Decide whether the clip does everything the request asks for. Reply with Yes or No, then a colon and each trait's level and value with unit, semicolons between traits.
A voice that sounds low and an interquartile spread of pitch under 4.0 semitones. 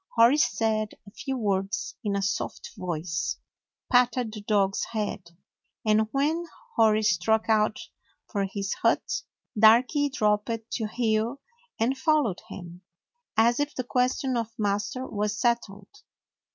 No: high, 220 Hz; average, 3.4 semitones